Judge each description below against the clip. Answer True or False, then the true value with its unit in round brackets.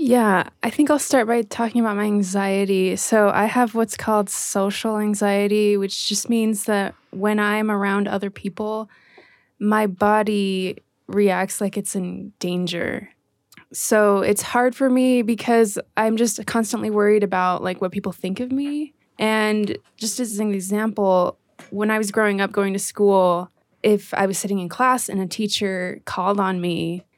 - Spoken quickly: False (165 wpm)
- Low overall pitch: False (210 Hz)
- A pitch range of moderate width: False (2.2 semitones)